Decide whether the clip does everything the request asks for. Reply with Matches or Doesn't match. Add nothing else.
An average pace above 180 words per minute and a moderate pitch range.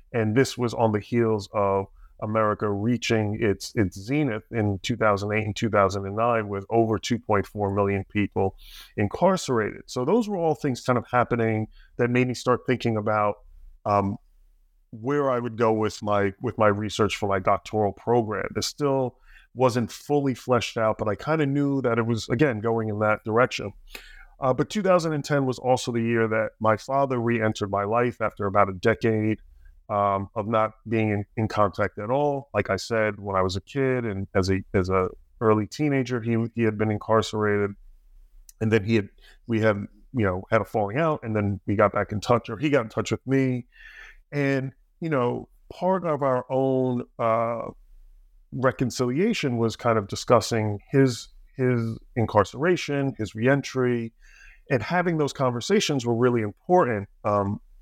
Doesn't match